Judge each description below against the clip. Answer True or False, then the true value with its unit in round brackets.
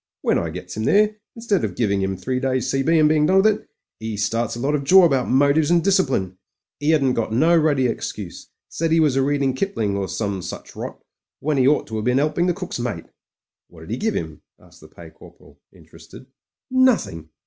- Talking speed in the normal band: False (220 wpm)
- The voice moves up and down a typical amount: False (7.0 semitones)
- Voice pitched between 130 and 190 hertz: True (135 Hz)